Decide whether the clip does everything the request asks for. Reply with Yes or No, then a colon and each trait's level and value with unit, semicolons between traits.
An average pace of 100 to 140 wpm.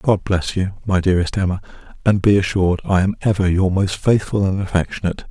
No: average, 190 wpm